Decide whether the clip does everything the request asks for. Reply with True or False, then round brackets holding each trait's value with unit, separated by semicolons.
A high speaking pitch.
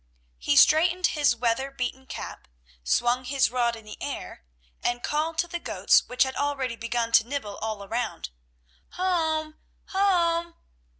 True (265 Hz)